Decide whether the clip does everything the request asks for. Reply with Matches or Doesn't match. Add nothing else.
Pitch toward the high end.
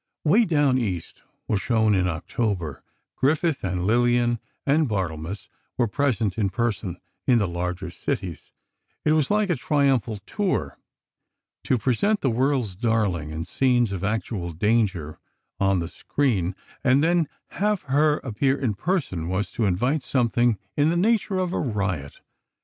Doesn't match